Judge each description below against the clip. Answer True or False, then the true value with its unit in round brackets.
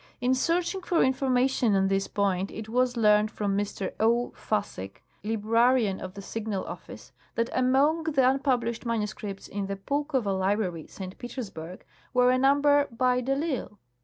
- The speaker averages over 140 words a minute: True (160 wpm)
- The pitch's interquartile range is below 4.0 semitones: False (4.6 semitones)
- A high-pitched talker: True (230 Hz)